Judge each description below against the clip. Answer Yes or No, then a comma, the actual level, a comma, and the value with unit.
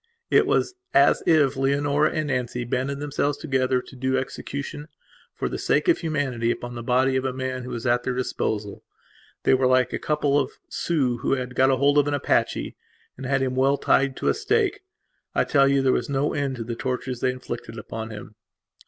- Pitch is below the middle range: Yes, low, 130 Hz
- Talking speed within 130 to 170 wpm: No, fast, 205 wpm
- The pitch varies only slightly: Yes, narrow, 2.1 semitones